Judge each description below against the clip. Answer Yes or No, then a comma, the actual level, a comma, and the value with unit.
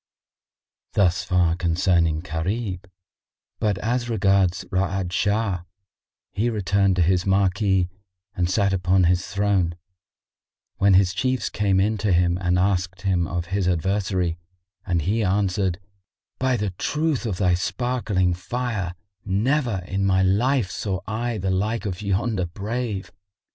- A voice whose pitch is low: Yes, very low, 95 Hz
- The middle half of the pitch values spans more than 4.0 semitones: No, average, 2.7 semitones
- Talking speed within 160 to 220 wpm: No, slow, 135 wpm